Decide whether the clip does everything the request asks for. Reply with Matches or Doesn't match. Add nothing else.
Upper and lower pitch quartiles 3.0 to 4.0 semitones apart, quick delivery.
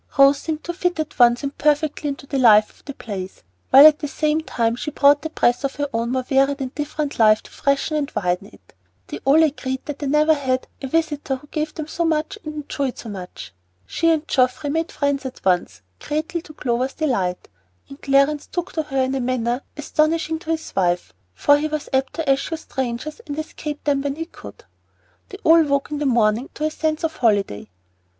Matches